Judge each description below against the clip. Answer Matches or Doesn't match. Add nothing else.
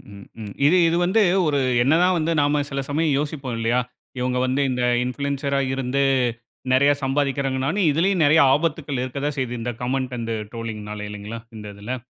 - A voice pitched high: Doesn't match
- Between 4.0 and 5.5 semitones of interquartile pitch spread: Doesn't match